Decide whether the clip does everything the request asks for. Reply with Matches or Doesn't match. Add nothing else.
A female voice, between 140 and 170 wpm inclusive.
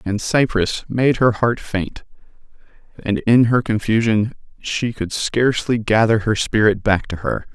Doesn't match